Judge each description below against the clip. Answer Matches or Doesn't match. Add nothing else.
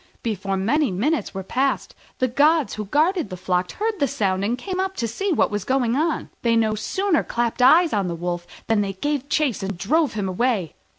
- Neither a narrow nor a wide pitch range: Doesn't match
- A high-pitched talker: Matches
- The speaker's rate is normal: Doesn't match